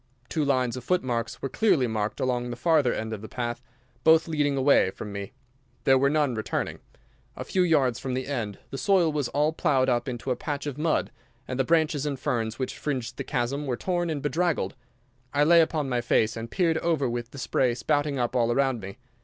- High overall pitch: No, low, 135 Hz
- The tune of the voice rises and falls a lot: No, average, 4.0 semitones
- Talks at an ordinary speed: No, fast, 215 wpm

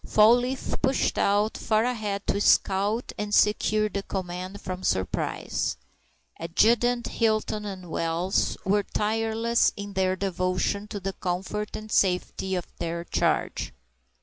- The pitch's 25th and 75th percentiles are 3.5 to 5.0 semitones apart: No, average, 2.7 semitones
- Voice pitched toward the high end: Yes, high, 205 Hz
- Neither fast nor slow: No, slow, 130 wpm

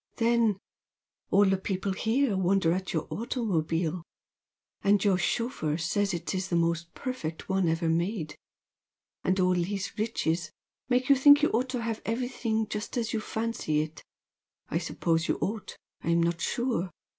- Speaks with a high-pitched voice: Yes, high, 195 Hz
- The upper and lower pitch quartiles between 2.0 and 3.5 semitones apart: No, average, 5.3 semitones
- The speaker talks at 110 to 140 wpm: No, average, 155 wpm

